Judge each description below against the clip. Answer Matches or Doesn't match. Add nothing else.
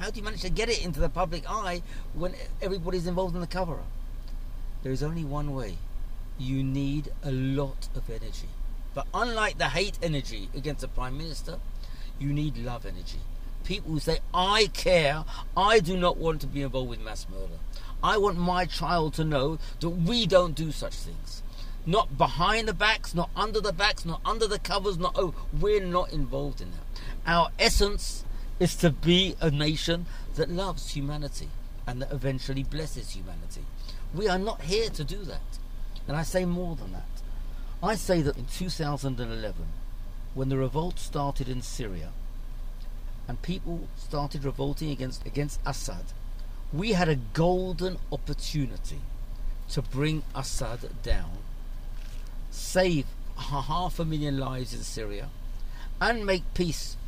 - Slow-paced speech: Doesn't match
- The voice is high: Doesn't match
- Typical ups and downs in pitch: Doesn't match